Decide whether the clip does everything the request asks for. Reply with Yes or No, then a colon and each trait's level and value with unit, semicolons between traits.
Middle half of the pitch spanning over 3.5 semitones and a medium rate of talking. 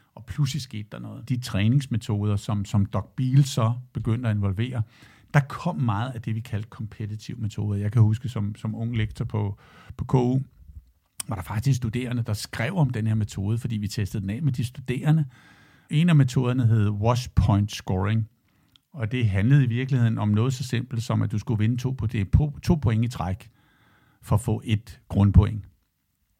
No: average, 3.2 semitones; average, 195 wpm